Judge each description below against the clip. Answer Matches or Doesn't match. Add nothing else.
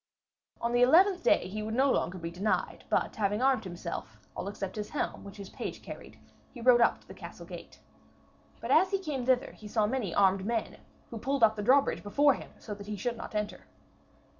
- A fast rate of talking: Matches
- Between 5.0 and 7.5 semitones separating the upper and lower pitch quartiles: Doesn't match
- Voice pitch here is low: Doesn't match